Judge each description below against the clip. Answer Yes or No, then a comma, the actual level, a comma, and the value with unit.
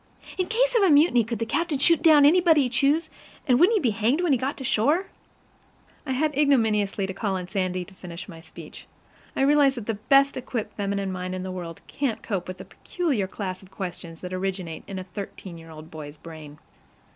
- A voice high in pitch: Yes, high, 215 Hz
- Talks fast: Yes, fast, 215 wpm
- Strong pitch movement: Yes, wide, 7.6 semitones